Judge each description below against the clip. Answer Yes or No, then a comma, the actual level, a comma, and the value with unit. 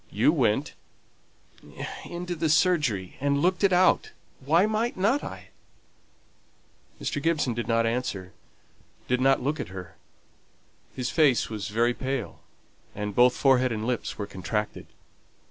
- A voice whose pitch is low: Yes, low, 130 Hz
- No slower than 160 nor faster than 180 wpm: No, average, 140 wpm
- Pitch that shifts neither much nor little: No, wide, 6.6 semitones